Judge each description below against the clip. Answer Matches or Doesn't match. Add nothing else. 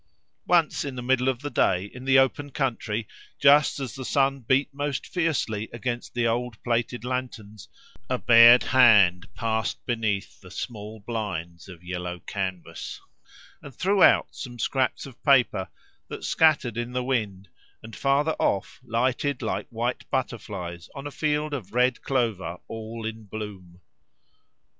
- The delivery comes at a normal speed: Matches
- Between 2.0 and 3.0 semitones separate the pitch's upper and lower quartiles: Doesn't match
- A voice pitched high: Doesn't match